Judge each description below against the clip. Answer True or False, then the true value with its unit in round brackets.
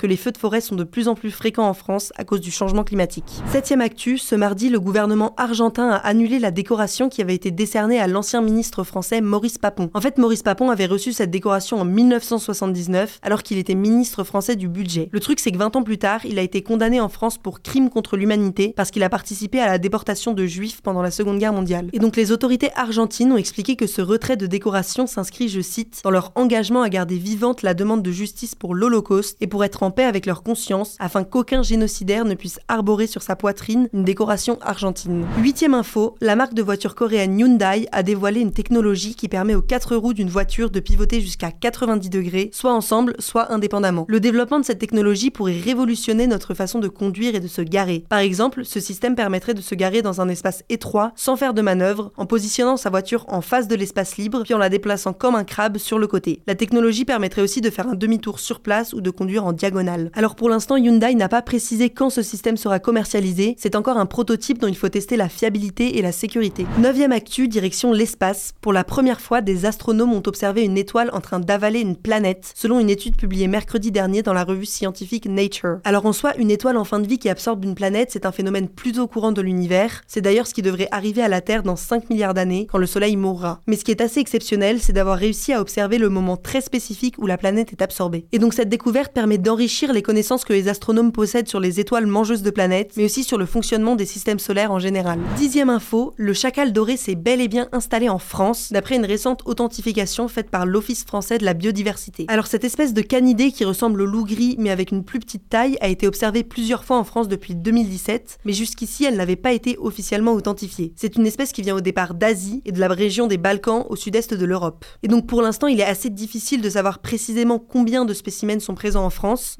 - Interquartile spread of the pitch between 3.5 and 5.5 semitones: False (3.1 semitones)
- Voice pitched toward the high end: True (215 Hz)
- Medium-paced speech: False (230 wpm)